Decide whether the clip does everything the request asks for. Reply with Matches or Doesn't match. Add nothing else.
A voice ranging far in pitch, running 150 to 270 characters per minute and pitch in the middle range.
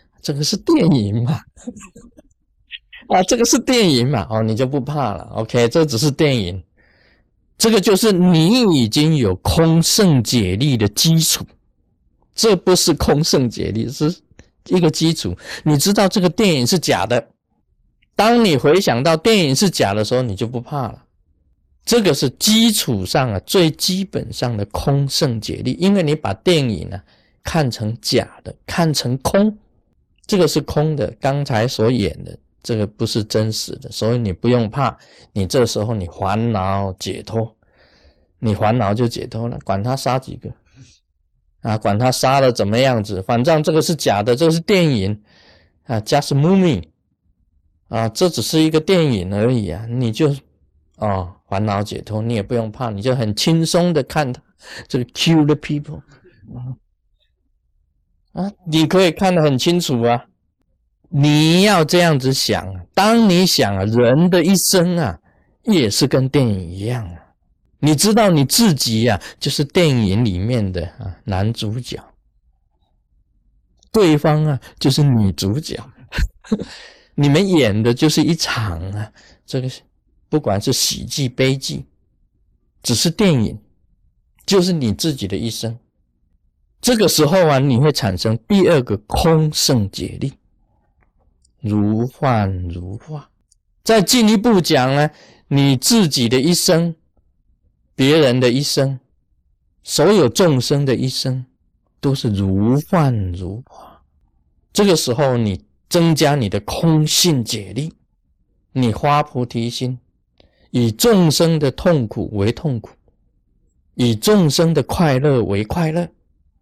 Doesn't match